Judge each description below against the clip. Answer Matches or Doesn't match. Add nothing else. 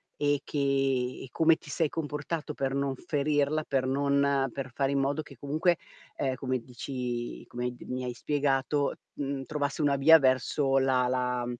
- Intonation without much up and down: Matches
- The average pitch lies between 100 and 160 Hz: Matches